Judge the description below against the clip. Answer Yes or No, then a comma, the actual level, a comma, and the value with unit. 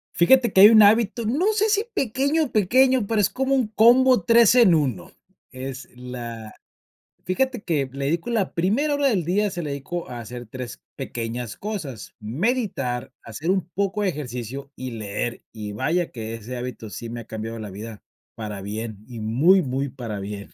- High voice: No, medium, 145 Hz